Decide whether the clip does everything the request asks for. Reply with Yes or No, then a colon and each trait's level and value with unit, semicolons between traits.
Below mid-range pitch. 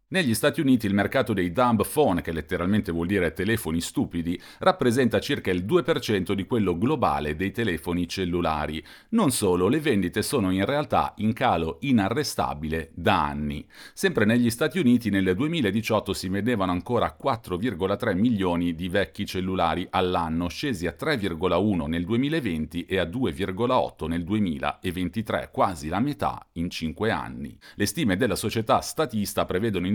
Yes: very low, 95 Hz